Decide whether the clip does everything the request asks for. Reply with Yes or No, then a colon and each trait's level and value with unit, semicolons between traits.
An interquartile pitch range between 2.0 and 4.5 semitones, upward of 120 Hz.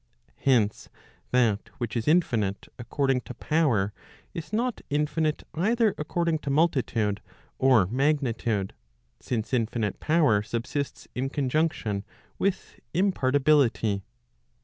No: wide, 5.5 semitones; low, 135 Hz